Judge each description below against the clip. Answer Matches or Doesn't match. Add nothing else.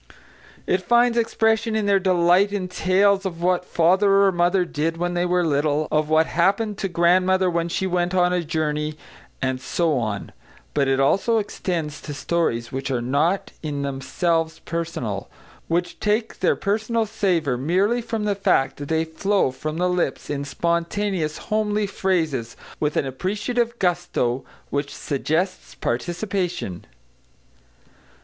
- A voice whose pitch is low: Doesn't match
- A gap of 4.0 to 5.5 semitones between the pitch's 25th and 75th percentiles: Matches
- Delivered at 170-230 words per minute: Doesn't match